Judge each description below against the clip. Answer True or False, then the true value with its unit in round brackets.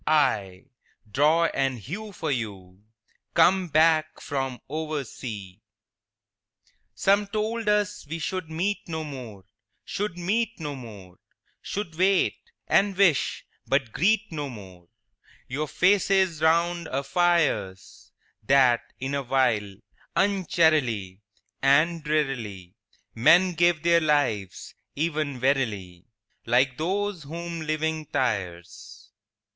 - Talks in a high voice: False (150 Hz)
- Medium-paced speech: False (110 wpm)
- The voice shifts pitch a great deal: True (6.3 semitones)